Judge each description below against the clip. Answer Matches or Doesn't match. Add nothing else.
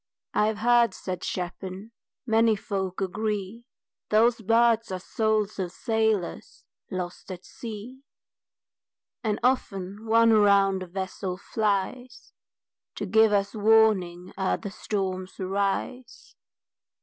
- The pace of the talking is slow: Matches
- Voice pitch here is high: Matches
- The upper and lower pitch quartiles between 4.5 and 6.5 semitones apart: Doesn't match